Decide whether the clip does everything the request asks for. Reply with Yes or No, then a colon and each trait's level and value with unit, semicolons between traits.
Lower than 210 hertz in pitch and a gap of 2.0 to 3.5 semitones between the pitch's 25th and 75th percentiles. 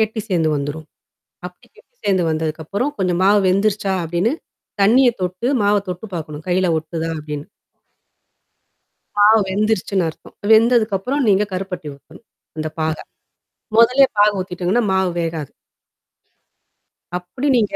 No: high, 190 Hz; average, 4.7 semitones